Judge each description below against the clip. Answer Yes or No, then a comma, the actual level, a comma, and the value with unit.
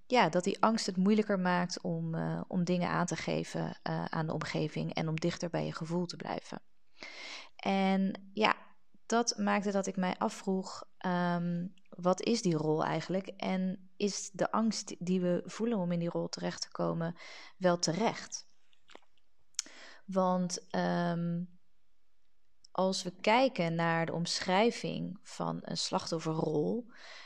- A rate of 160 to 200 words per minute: No, average, 150 wpm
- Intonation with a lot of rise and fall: No, average, 3.0 semitones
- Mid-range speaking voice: Yes, medium, 180 Hz